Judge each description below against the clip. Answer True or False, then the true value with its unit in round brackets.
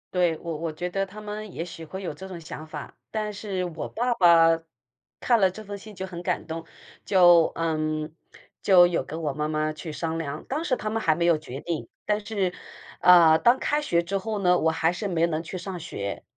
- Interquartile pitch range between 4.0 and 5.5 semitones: False (3.4 semitones)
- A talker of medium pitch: True (175 Hz)